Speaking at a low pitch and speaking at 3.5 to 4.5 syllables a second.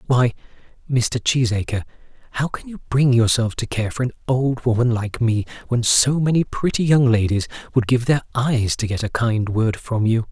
No: low, 120 Hz; 4.9 syllables/s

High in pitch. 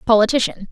Yes: high, 225 Hz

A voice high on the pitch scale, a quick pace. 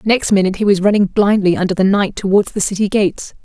Yes: high, 200 Hz; fast, 225 wpm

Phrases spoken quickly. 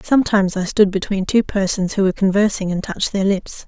Yes: fast, 210 wpm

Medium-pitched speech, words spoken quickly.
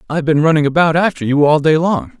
Yes: medium, 155 Hz; fast, 245 wpm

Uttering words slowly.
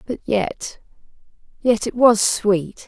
Yes: slow, 105 wpm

